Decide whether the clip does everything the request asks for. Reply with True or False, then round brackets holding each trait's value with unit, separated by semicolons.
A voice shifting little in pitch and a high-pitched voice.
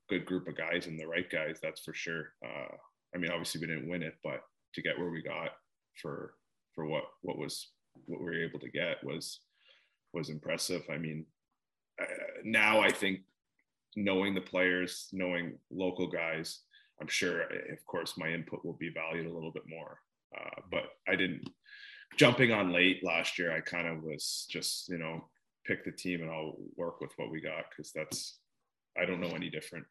False (1.9 semitones; 85 Hz)